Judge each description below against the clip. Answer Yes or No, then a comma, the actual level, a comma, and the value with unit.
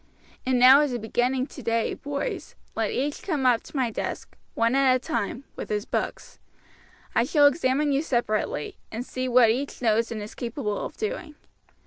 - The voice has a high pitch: Yes, very high, 255 Hz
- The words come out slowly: No, average, 180 wpm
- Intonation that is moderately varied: Yes, average, 3.2 semitones